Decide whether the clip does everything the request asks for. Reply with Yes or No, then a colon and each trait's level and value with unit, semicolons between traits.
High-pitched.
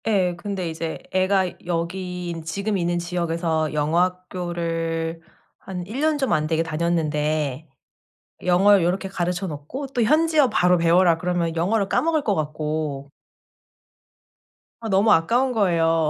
No: medium, 175 Hz